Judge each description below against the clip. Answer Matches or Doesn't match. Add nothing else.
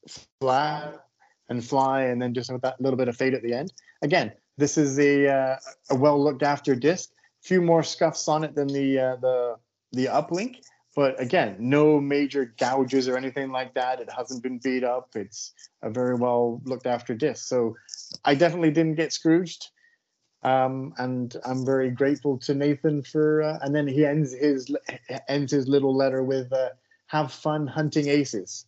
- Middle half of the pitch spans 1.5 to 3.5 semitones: Matches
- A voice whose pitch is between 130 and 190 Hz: Matches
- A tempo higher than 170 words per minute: Matches